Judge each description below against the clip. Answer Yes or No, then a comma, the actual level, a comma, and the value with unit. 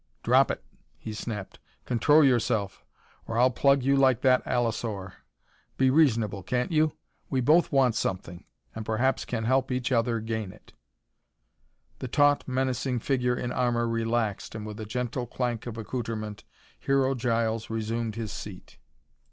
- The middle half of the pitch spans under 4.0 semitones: Yes, average, 2.7 semitones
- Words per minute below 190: Yes, average, 150 wpm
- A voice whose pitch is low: Yes, low, 120 Hz